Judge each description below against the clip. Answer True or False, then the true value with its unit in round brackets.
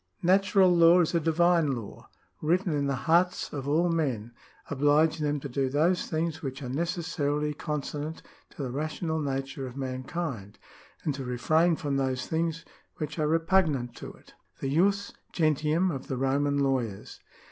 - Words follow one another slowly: False (170 wpm)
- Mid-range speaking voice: True (150 Hz)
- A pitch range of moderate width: True (3.5 semitones)